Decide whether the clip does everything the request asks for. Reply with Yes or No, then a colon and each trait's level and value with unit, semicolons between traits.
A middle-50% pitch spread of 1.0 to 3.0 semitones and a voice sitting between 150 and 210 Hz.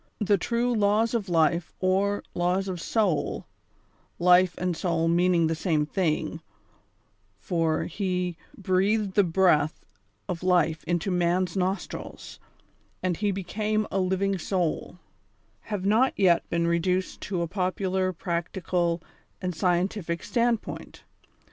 Yes: narrow, 2.5 semitones; medium, 185 Hz